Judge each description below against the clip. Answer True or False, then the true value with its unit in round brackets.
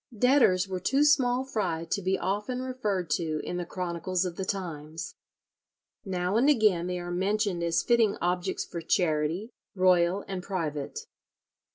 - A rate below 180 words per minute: True (155 wpm)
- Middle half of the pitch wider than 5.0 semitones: False (3.6 semitones)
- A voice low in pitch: False (185 Hz)